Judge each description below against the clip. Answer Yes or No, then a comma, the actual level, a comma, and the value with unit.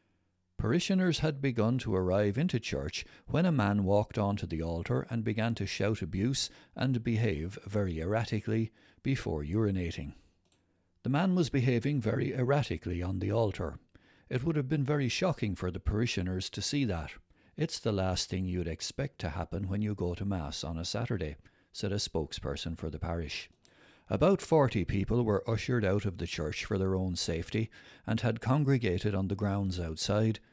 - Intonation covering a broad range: No, average, 4.8 semitones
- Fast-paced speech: No, average, 175 wpm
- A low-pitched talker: Yes, low, 100 Hz